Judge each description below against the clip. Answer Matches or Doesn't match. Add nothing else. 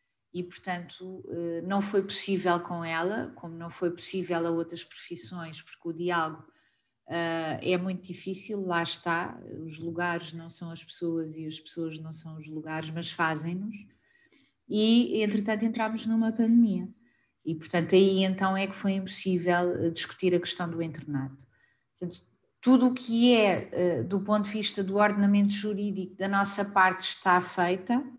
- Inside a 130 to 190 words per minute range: Matches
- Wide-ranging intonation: Doesn't match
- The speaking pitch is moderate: Matches